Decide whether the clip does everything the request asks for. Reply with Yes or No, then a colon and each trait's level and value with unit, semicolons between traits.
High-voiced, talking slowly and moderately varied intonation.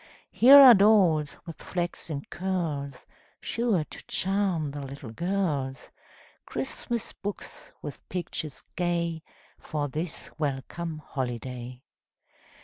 No: medium, 160 Hz; slow, 100 wpm; average, 5.0 semitones